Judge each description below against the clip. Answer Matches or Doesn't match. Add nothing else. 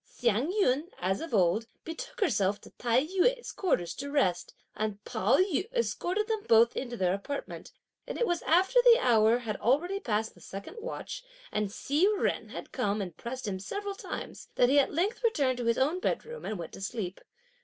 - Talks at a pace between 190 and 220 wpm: Matches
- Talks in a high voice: Matches